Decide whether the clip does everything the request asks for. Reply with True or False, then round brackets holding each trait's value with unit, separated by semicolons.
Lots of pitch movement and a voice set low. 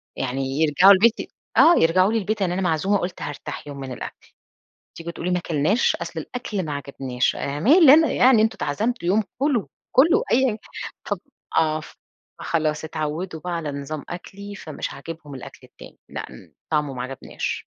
False (6.2 semitones; 175 Hz)